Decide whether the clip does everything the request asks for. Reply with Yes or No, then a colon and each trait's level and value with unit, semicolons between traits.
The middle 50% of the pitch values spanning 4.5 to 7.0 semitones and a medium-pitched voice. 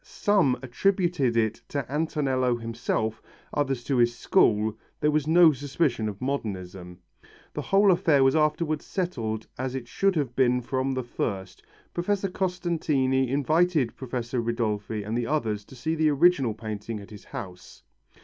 No: average, 5.2 semitones; low, 130 Hz